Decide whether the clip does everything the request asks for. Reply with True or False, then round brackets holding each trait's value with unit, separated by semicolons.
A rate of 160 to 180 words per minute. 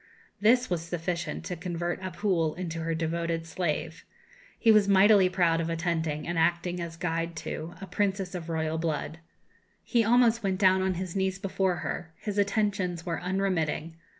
True (165 wpm)